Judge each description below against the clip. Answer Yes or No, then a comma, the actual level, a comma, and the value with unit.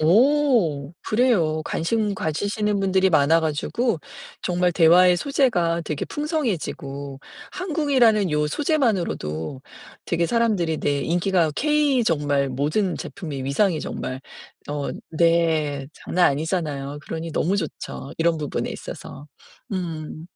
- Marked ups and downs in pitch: Yes, wide, 5.8 semitones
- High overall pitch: No, medium, 170 Hz